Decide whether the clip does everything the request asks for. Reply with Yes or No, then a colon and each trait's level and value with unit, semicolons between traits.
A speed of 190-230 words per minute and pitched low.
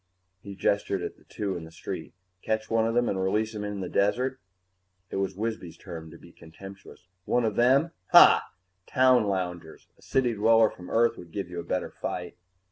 Yes: average, 200 wpm; low, 100 Hz